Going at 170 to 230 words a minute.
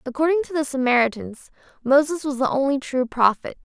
No: average, 160 wpm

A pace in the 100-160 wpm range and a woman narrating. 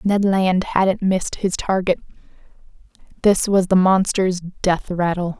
Yes: slow, 135 wpm; female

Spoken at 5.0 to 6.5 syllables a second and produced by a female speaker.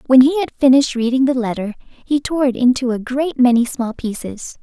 Yes: 5.3 syllables/s; female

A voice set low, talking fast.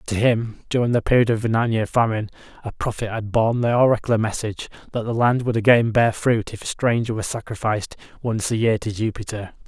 Yes: low, 110 Hz; fast, 210 wpm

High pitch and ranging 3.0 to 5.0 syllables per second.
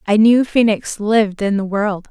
Yes: high, 210 Hz; 4.7 syllables/s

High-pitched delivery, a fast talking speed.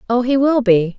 Yes: high, 235 Hz; fast, 245 wpm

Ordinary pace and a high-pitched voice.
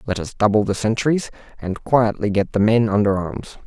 No: average, 195 wpm; low, 105 Hz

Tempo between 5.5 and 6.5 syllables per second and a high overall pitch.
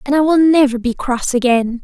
No: 5.2 syllables/s; very high, 265 Hz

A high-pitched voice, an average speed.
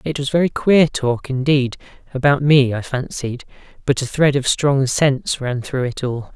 No: low, 135 Hz; average, 170 wpm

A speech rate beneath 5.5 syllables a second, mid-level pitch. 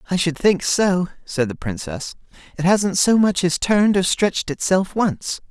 Yes: 4.6 syllables/s; medium, 180 Hz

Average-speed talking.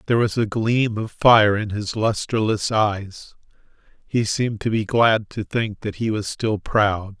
Yes: average, 185 wpm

